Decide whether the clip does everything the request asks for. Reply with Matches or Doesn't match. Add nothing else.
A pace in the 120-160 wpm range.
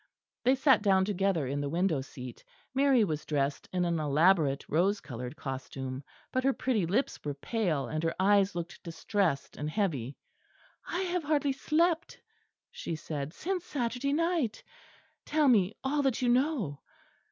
Matches